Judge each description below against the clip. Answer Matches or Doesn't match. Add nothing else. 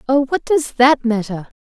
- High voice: Matches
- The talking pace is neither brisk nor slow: Matches